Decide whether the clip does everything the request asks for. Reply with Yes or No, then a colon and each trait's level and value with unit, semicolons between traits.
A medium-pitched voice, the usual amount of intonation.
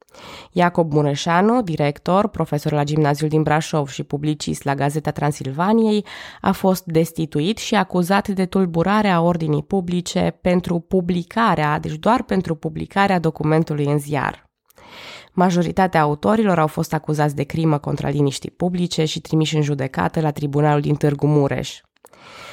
Yes: medium, 160 Hz; average, 3.6 semitones